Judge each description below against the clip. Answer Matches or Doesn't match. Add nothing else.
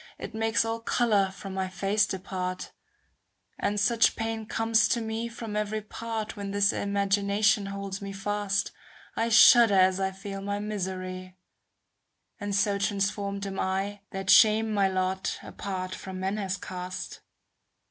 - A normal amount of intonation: Doesn't match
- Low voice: Doesn't match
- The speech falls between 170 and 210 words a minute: Doesn't match